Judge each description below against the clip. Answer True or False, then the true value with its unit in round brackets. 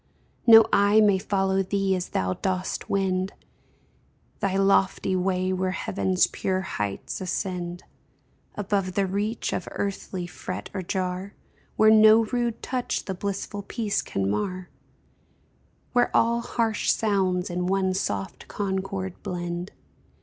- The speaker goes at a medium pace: False (130 wpm)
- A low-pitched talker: False (190 Hz)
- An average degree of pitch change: False (1.8 semitones)